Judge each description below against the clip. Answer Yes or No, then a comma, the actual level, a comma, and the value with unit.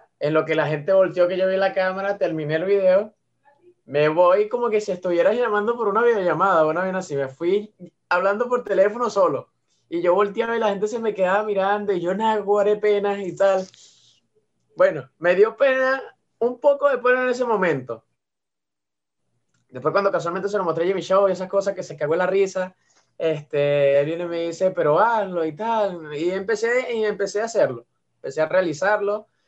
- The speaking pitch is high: Yes, high, 195 Hz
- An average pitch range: Yes, average, 3.9 semitones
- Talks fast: Yes, fast, 195 wpm